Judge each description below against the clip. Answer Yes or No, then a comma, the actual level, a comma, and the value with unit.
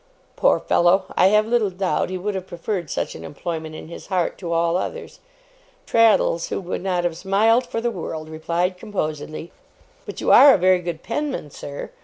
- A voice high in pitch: No, medium, 180 Hz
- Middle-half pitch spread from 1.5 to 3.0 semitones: No, average, 3.8 semitones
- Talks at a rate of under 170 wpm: No, average, 190 wpm